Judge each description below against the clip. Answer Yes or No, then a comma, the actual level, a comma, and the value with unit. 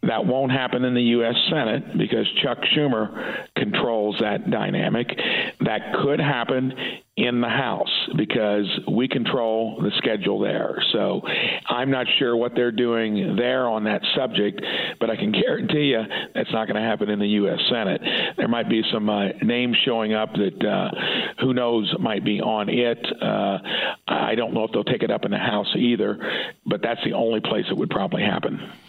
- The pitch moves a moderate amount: No, narrow, 2.2 semitones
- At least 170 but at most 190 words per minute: Yes, average, 185 wpm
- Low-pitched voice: Yes, low, 120 Hz